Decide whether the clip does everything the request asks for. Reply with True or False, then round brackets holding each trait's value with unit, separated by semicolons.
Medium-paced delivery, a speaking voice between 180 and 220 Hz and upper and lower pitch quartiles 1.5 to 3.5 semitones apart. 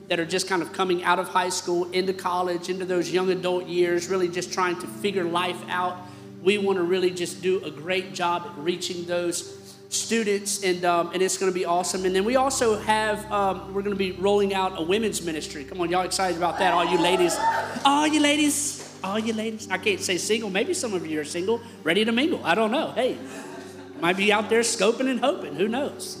False (230 wpm; 185 Hz; 2.6 semitones)